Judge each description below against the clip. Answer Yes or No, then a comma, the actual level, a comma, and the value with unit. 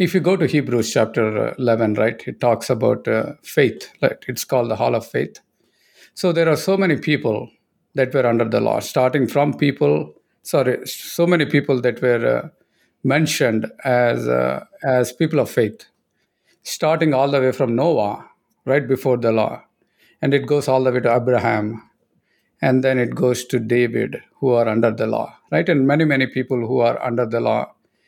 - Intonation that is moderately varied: Yes, average, 3.5 semitones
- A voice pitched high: No, low, 130 Hz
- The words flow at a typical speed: Yes, average, 185 wpm